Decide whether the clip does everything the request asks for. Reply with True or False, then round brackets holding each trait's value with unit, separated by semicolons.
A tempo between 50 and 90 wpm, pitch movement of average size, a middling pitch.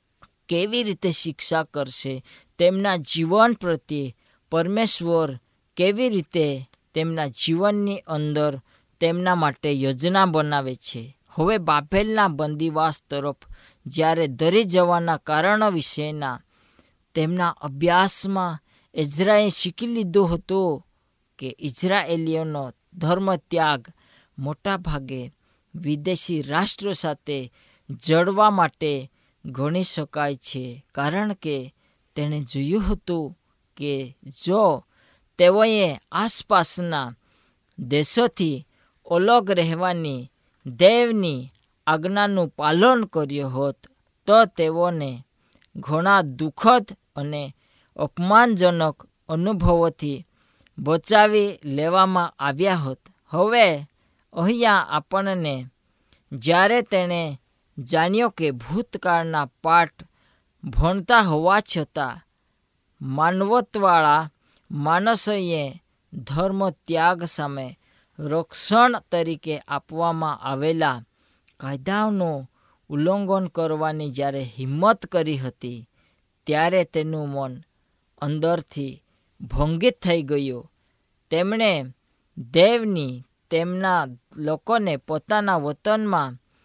True (80 wpm; 4.8 semitones; 160 Hz)